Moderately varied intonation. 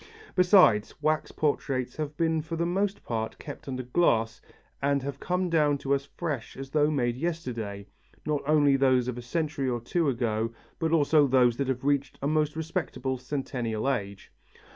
Yes: average, 4.0 semitones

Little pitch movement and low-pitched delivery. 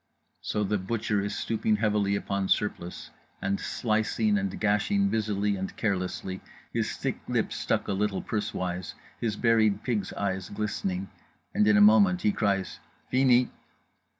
Yes: narrow, 1.8 semitones; low, 105 Hz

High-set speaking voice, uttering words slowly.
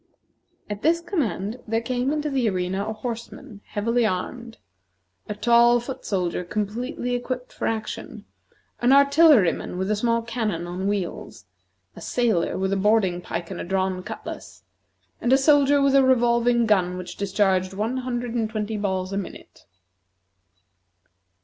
No: high, 225 Hz; average, 150 wpm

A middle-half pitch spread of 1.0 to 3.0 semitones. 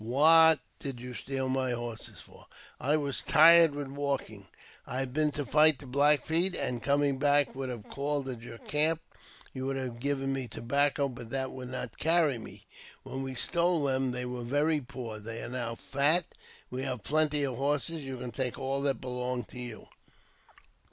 Yes: narrow, 2.6 semitones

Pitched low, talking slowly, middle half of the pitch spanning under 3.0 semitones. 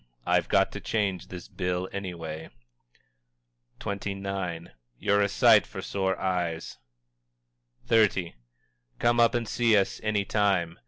Yes: very low, 95 Hz; slow, 120 wpm; narrow, 2.5 semitones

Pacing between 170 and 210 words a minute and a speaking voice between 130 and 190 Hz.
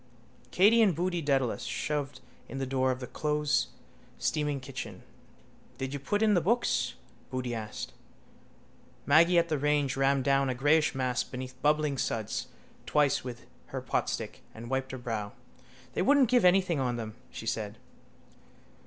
No: average, 155 wpm; medium, 140 Hz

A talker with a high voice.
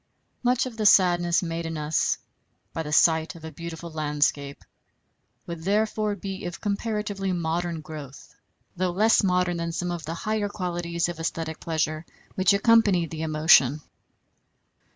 No: medium, 170 Hz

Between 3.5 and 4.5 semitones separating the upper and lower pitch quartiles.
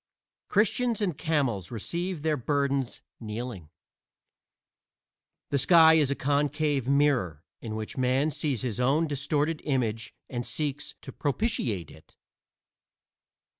Yes: average, 4.2 semitones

